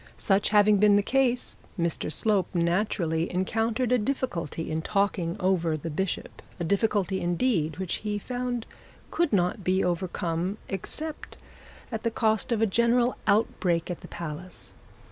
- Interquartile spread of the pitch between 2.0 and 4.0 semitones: No, average, 4.4 semitones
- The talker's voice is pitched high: Yes, high, 195 Hz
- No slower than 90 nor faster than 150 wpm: Yes, average, 145 wpm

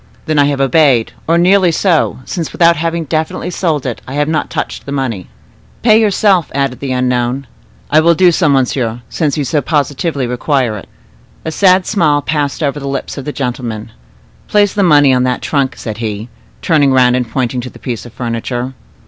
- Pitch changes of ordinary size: Yes, average, 4.5 semitones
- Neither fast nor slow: Yes, average, 190 wpm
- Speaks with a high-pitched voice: No, medium, 140 Hz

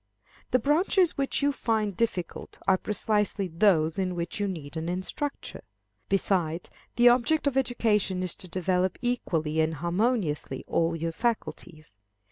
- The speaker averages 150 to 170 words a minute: No, average, 140 wpm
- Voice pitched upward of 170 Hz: Yes, high, 190 Hz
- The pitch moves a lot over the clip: Yes, wide, 6.0 semitones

